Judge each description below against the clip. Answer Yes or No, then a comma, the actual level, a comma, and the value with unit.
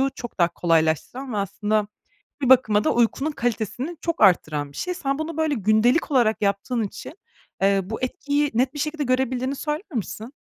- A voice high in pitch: Yes, high, 245 Hz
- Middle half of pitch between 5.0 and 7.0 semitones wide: Yes, wide, 5.5 semitones